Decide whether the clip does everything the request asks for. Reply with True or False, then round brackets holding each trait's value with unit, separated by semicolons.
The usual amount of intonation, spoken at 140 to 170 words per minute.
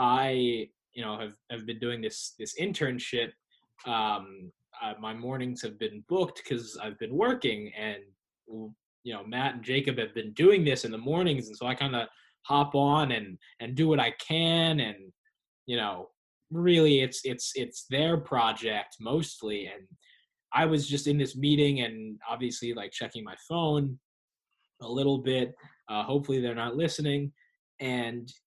True (4.5 semitones; 165 wpm)